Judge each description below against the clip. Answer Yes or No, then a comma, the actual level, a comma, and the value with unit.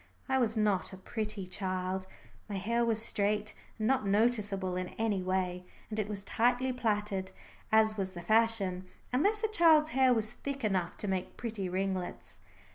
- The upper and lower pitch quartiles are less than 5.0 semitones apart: Yes, average, 3.7 semitones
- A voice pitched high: Yes, high, 210 Hz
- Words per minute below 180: Yes, average, 170 wpm